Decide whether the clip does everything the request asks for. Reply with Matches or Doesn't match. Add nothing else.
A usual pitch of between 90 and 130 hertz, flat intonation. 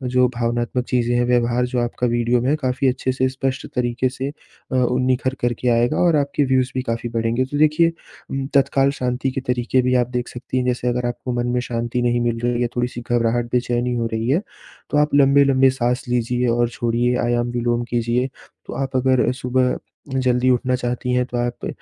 Matches